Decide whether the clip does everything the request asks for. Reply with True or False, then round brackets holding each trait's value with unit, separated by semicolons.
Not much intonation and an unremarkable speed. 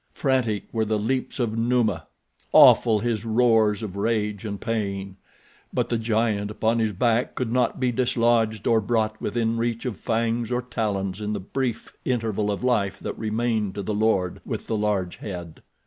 True (2.2 semitones; 170 wpm)